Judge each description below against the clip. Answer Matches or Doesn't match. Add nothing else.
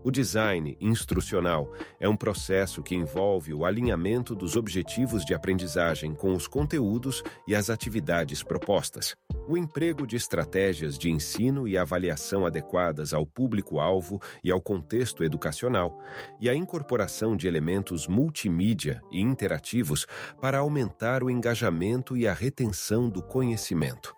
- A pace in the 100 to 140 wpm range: Matches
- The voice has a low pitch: Matches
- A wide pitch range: Matches